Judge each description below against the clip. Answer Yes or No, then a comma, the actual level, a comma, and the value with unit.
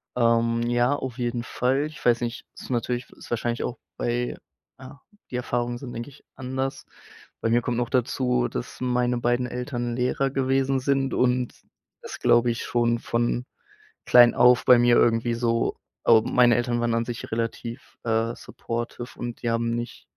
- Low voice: Yes, low, 120 Hz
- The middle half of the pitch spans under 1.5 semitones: Yes, narrow, 1.1 semitones